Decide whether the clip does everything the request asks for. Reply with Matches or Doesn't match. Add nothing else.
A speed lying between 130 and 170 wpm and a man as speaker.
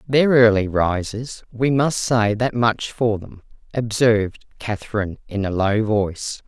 Doesn't match